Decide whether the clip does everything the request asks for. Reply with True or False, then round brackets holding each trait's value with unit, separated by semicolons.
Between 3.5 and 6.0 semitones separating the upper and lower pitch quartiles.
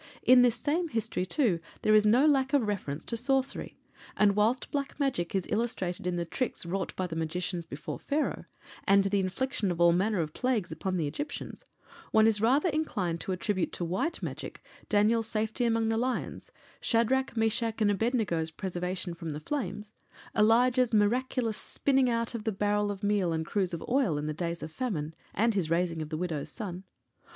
True (5.3 semitones)